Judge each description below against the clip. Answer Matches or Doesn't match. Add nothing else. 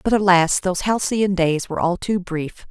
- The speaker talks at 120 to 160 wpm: Doesn't match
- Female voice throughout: Matches